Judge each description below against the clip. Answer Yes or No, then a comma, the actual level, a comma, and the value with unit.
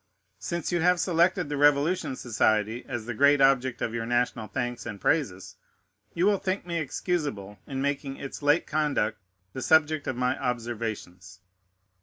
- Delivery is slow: No, average, 160 wpm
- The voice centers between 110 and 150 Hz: Yes, low, 135 Hz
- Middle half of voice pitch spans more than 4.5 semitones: Yes, average, 5.1 semitones